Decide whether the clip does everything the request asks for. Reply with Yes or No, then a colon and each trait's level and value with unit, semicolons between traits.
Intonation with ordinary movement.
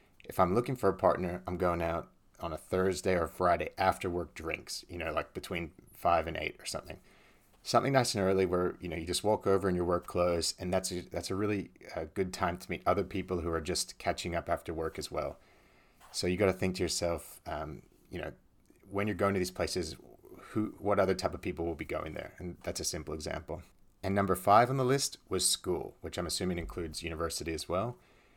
No: narrow, 2.1 semitones